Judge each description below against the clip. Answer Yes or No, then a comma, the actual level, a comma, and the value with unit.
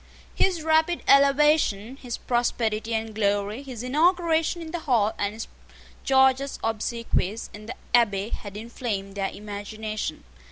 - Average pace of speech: No, slow, 130 wpm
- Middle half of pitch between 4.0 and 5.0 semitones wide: Yes, average, 4.7 semitones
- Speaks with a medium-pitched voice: No, high, 230 Hz